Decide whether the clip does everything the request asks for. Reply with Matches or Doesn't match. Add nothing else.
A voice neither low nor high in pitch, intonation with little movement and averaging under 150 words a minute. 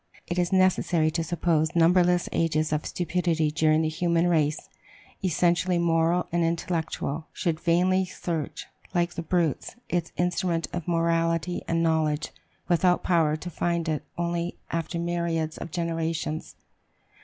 Matches